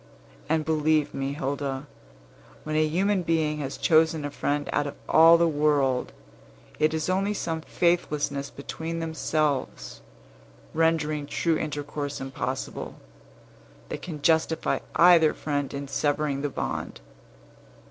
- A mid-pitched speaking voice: Yes, medium, 150 Hz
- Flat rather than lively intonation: Yes, narrow, 2.2 semitones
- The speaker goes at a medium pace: No, slow, 125 wpm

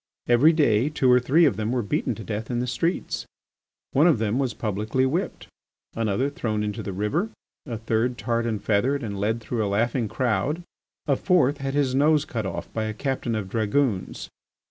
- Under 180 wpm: No, average, 195 wpm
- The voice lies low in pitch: Yes, low, 120 Hz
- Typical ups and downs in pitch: Yes, average, 4.3 semitones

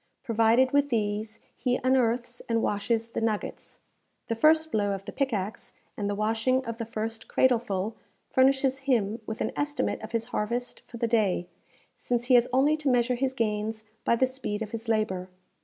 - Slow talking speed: No, average, 180 wpm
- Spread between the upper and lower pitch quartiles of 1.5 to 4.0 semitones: Yes, average, 3.0 semitones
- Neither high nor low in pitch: No, high, 230 Hz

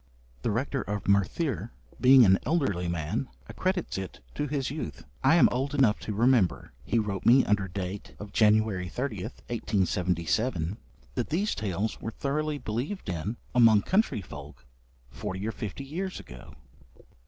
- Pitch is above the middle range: No, low, 110 Hz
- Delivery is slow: No, average, 150 wpm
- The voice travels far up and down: Yes, wide, 6.1 semitones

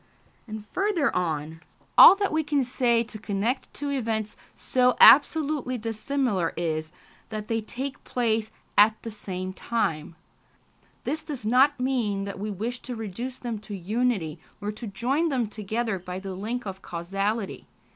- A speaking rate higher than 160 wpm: No, average, 155 wpm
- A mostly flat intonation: No, average, 4.3 semitones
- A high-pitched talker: Yes, high, 220 Hz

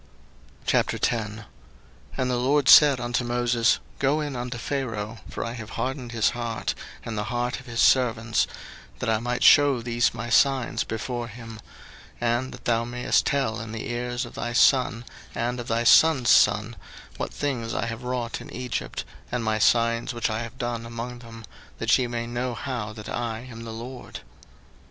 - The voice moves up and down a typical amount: No, narrow, 1.5 semitones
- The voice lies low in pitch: Yes, low, 120 Hz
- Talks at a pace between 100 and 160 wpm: No, average, 180 wpm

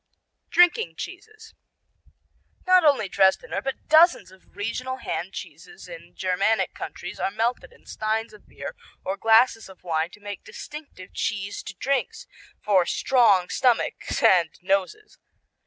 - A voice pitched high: Yes, high, 220 Hz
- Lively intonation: Yes, wide, 6.8 semitones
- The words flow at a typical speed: No, slow, 130 wpm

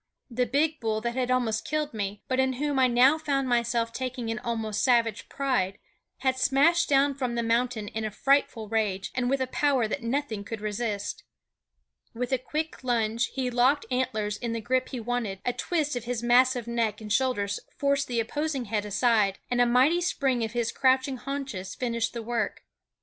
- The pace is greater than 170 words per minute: Yes, average, 195 wpm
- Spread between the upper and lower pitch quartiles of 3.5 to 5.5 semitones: No, average, 2.8 semitones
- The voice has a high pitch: Yes, high, 245 Hz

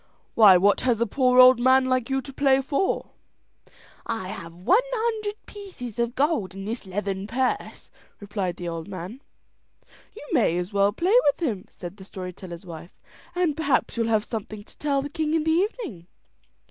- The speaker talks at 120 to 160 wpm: No, average, 185 wpm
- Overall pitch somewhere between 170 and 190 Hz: No, high, 235 Hz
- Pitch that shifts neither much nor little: No, wide, 6.8 semitones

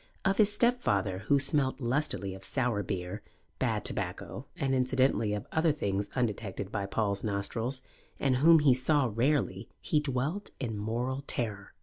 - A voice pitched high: No, low, 125 Hz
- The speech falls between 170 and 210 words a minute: No, average, 150 wpm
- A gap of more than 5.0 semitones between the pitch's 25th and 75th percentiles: Yes, wide, 5.5 semitones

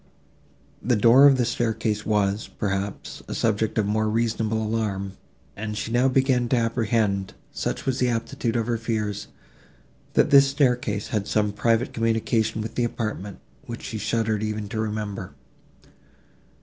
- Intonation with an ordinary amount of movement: No, narrow, 1.9 semitones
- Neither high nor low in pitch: No, low, 110 Hz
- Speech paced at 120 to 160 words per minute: Yes, average, 150 wpm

